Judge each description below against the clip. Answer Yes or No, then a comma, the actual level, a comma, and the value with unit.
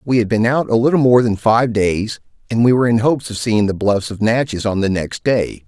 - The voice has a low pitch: Yes, low, 115 Hz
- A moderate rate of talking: No, fast, 265 wpm